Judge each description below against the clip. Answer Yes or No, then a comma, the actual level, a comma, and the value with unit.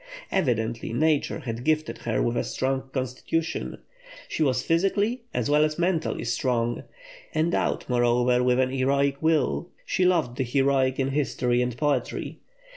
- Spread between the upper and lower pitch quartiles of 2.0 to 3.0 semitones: No, average, 4.1 semitones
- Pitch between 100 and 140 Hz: Yes, low, 135 Hz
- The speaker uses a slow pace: No, average, 145 wpm